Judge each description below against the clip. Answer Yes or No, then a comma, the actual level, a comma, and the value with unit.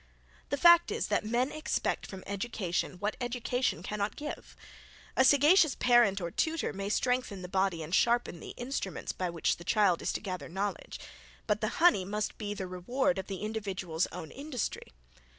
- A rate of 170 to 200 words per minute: Yes, average, 175 wpm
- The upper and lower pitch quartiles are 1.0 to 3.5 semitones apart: No, average, 5.1 semitones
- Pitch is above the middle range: Yes, high, 210 Hz